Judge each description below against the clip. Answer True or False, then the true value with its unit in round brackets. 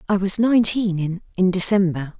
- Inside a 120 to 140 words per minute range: True (135 wpm)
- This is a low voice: False (190 Hz)